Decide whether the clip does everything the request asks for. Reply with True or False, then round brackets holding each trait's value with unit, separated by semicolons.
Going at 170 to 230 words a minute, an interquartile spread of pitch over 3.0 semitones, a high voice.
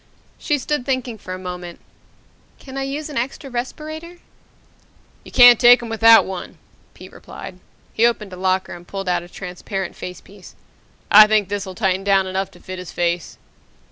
True (175 wpm; 4.9 semitones; 200 Hz)